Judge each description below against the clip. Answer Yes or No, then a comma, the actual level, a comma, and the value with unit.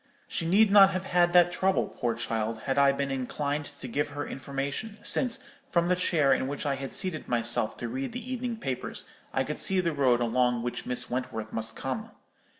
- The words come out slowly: No, fast, 205 wpm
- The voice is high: No, medium, 140 Hz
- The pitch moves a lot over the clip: Yes, wide, 6.4 semitones